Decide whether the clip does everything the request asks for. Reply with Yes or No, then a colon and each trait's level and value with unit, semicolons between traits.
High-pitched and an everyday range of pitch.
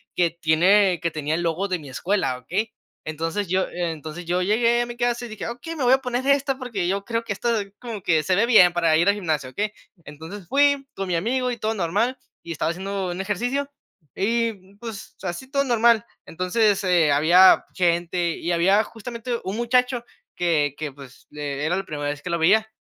No: high, 195 Hz; wide, 5.7 semitones